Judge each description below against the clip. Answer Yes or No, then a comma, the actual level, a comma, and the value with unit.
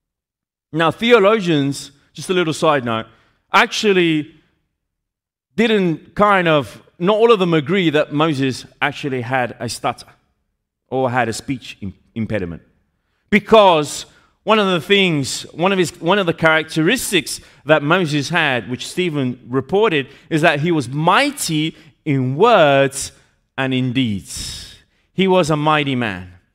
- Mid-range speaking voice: Yes, medium, 150 Hz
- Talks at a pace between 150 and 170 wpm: No, average, 135 wpm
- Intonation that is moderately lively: No, wide, 6.0 semitones